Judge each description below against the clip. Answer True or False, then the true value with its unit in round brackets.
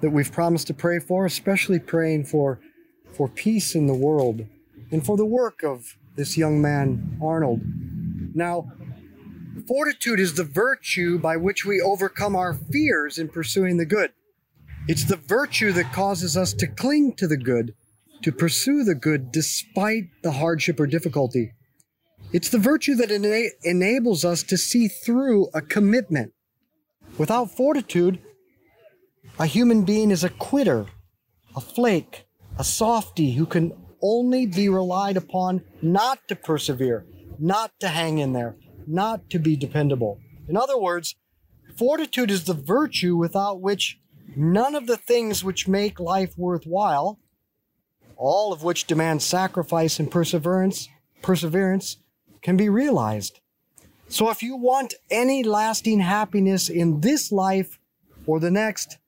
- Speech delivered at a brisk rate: False (145 wpm)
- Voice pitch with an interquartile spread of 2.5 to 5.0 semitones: False (5.4 semitones)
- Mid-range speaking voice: True (180 Hz)